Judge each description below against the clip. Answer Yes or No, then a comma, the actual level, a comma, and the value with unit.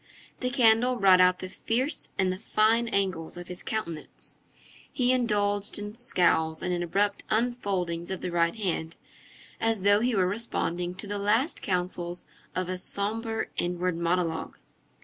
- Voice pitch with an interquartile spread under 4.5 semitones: Yes, average, 3.9 semitones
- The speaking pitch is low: No, high, 195 Hz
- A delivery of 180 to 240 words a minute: No, average, 155 wpm